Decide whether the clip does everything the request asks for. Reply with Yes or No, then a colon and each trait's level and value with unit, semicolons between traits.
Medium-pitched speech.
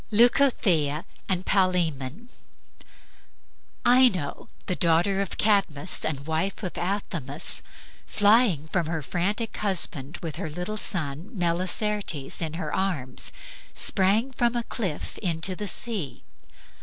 Yes: medium, 180 Hz